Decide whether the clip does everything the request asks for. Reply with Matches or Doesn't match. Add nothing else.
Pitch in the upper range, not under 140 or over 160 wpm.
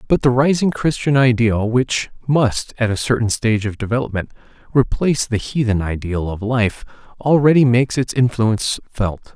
Doesn't match